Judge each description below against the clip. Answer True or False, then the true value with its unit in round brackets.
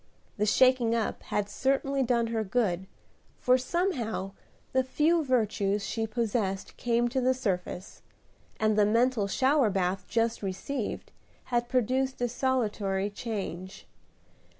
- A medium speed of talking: False (125 wpm)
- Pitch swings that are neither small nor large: True (4.1 semitones)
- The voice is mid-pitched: False (230 Hz)